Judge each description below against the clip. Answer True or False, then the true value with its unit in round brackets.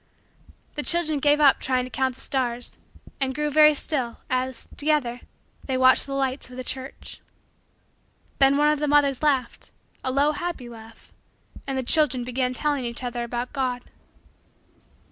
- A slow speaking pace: False (165 wpm)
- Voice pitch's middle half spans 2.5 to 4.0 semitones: True (2.8 semitones)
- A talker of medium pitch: False (265 Hz)